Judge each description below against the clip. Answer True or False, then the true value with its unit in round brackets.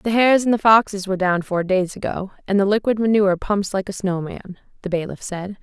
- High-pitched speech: True (195 Hz)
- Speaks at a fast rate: True (225 wpm)